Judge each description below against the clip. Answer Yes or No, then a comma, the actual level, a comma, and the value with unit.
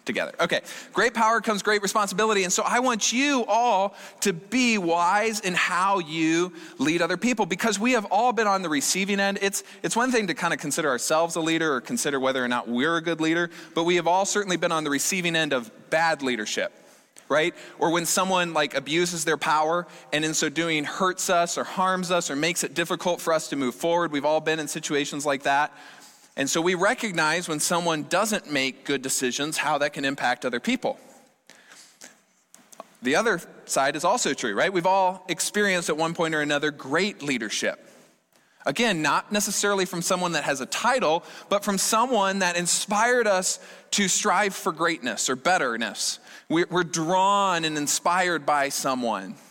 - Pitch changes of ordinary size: Yes, average, 4.1 semitones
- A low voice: No, medium, 175 Hz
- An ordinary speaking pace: Yes, average, 190 wpm